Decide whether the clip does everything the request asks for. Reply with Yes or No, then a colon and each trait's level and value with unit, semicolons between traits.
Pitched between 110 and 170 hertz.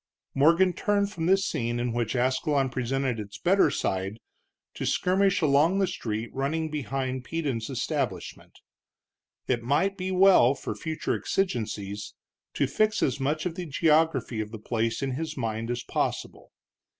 Yes: low, 135 Hz